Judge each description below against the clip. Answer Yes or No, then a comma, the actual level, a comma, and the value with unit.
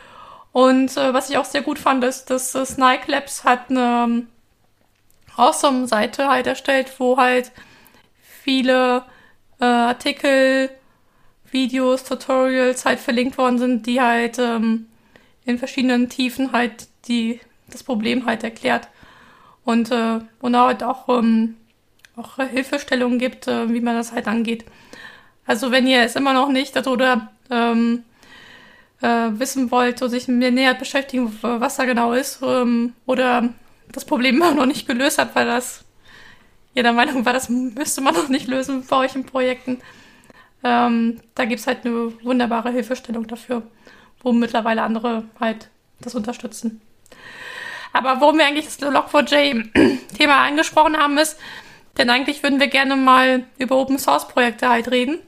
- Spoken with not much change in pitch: Yes, narrow, 1.8 semitones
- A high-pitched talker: Yes, very high, 255 Hz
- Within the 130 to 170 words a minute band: Yes, average, 150 wpm